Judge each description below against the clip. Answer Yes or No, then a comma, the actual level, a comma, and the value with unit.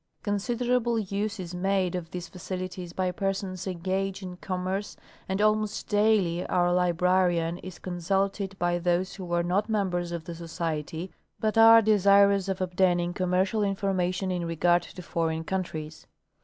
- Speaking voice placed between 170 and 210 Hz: Yes, medium, 185 Hz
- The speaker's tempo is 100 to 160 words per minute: Yes, average, 145 wpm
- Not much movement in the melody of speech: Yes, narrow, 2.2 semitones